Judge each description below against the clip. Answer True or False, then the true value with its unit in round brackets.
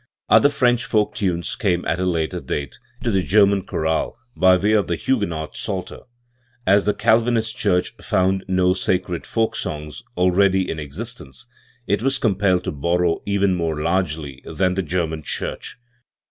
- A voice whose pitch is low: True (95 Hz)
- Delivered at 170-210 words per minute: False (160 wpm)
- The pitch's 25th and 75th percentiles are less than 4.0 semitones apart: True (3.4 semitones)